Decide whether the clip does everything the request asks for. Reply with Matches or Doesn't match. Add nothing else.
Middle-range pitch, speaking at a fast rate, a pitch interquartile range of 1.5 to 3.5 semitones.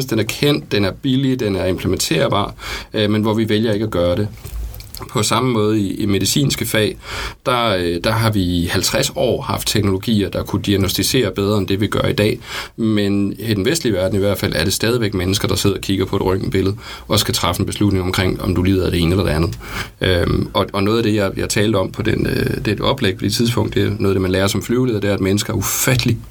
Doesn't match